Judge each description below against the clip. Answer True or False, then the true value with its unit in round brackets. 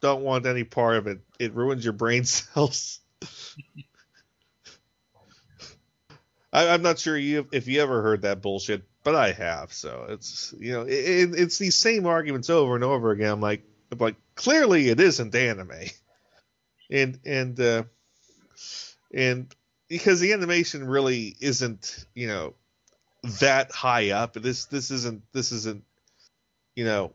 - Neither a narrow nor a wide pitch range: True (4.0 semitones)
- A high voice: False (125 Hz)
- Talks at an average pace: True (150 wpm)